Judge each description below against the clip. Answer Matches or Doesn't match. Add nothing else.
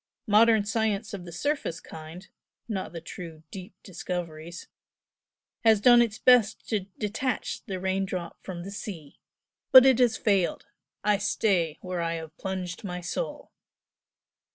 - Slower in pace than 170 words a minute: Matches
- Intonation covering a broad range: Doesn't match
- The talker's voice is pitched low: Doesn't match